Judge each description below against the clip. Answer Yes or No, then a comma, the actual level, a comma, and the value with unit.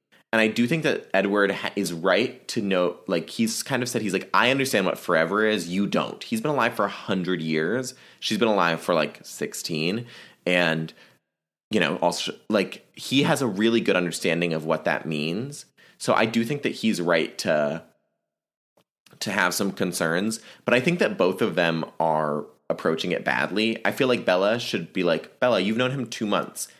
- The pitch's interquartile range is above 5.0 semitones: Yes, wide, 5.5 semitones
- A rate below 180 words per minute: No, average, 195 wpm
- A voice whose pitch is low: Yes, low, 100 Hz